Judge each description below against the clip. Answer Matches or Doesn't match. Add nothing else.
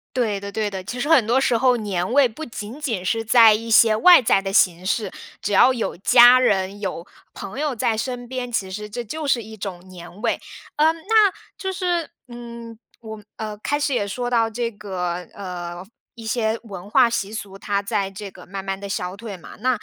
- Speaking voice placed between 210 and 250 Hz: Matches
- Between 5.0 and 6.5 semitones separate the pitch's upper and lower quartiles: Doesn't match